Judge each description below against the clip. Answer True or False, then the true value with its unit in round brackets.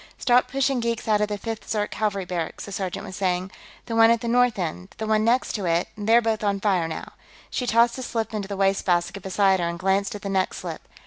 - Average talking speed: False (250 wpm)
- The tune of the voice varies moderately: True (3.2 semitones)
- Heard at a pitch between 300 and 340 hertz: False (205 Hz)